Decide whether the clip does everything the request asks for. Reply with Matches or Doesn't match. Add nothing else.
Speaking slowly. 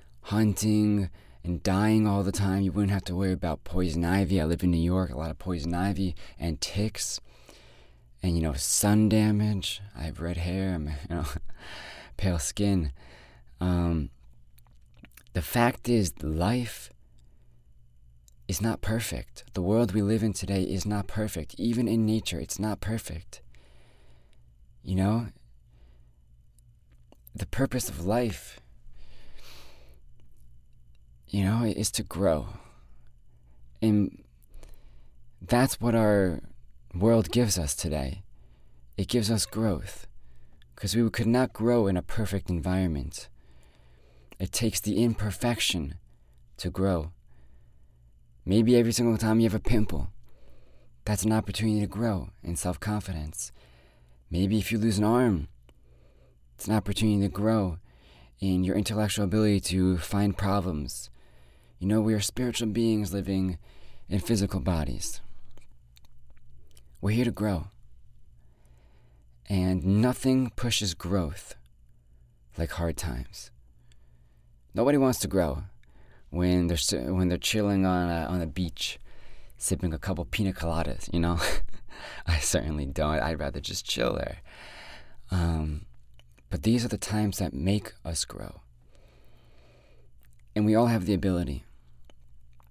Matches